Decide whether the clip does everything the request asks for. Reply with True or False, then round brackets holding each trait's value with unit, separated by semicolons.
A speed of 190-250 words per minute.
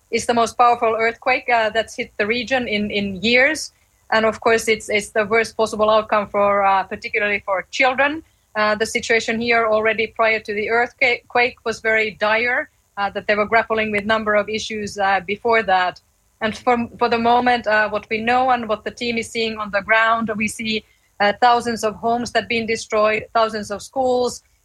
True (200 wpm)